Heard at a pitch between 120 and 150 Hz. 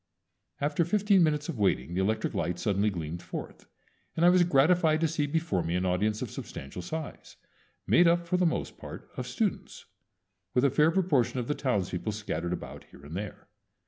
Yes: low, 135 Hz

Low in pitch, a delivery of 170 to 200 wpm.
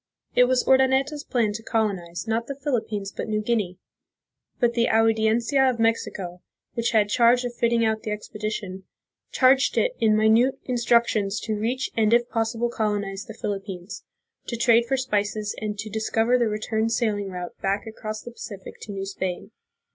No: high, 220 Hz; average, 175 wpm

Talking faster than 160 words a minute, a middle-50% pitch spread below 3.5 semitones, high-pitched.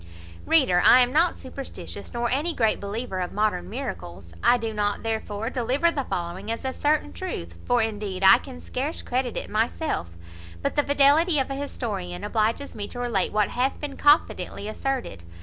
No: average, 180 wpm; average, 5.0 semitones; high, 235 Hz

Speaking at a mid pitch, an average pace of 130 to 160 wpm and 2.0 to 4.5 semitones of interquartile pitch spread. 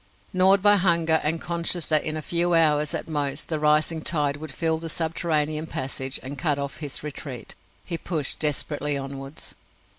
No: medium, 155 Hz; average, 175 wpm; narrow, 2.4 semitones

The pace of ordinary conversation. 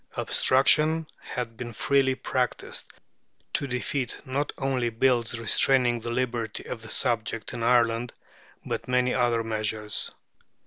No: slow, 125 wpm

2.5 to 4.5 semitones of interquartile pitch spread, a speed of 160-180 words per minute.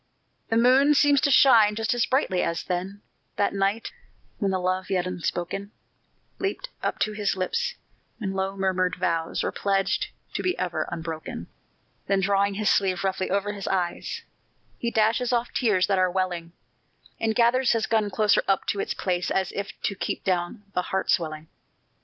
Yes: average, 3.3 semitones; average, 175 wpm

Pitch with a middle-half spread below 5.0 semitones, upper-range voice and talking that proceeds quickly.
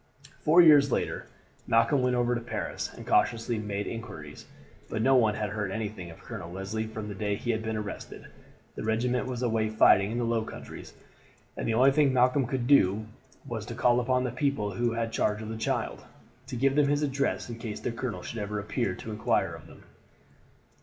No: average, 2.9 semitones; low, 115 Hz; fast, 210 wpm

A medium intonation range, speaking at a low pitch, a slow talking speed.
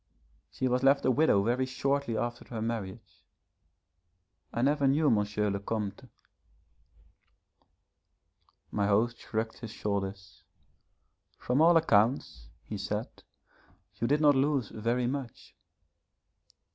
Yes: average, 4.5 semitones; low, 115 Hz; slow, 115 wpm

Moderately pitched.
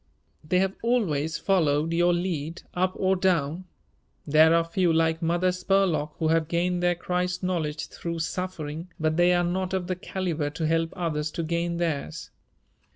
Yes: medium, 170 Hz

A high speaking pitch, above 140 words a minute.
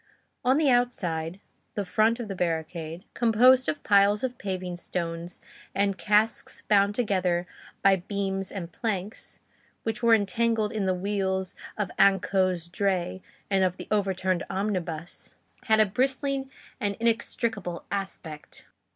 No: high, 200 Hz; slow, 135 wpm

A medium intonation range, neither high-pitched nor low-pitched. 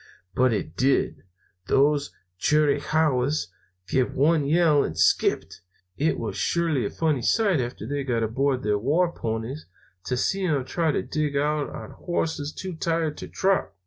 Yes: average, 3.9 semitones; medium, 145 Hz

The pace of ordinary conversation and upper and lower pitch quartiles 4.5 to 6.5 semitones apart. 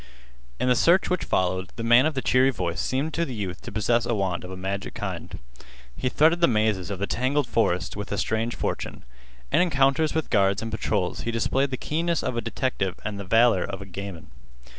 No: fast, 220 wpm; average, 5.3 semitones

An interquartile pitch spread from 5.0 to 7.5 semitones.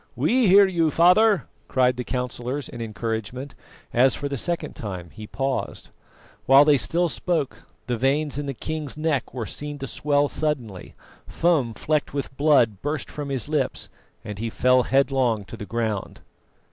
No: average, 4.3 semitones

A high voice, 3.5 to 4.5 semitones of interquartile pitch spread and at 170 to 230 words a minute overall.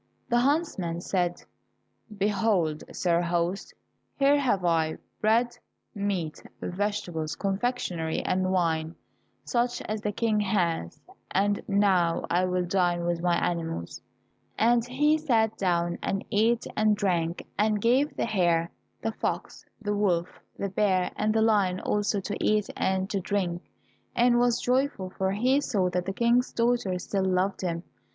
No: high, 195 Hz; average, 4.0 semitones; average, 145 wpm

